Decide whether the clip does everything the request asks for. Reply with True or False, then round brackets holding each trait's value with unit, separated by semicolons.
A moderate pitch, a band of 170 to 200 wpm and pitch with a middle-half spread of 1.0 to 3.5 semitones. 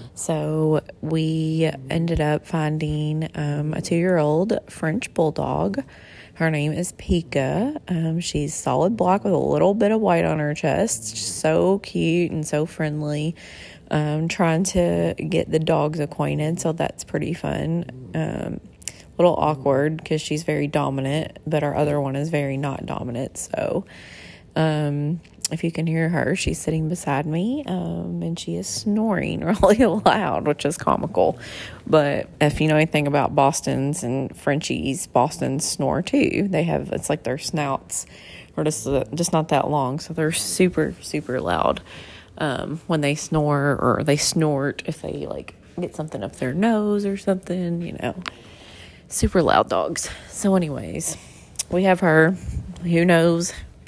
False (155 Hz; 155 wpm; 2.6 semitones)